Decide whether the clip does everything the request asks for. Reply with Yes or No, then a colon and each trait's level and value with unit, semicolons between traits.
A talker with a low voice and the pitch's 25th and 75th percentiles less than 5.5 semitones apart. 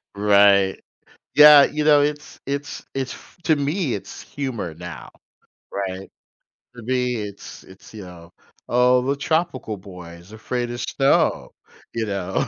No: low, 120 Hz; wide, 6.1 semitones